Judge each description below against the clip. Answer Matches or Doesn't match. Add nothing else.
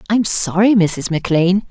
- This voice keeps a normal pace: Matches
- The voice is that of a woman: Matches